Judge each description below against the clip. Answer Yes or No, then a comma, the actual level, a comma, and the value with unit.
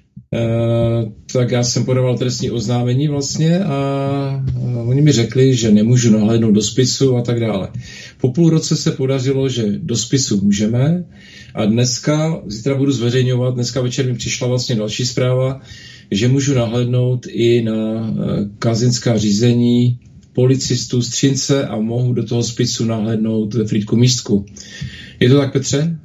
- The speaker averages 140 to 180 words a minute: Yes, average, 145 wpm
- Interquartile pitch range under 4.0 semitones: Yes, narrow, 2.6 semitones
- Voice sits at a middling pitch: No, low, 125 Hz